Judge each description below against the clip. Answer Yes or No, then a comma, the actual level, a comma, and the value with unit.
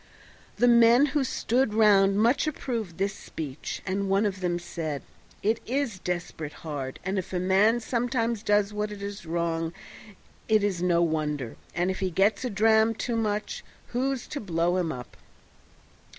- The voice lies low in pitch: No, high, 200 Hz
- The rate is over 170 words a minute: No, average, 165 wpm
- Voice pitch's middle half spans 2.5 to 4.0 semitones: No, average, 4.6 semitones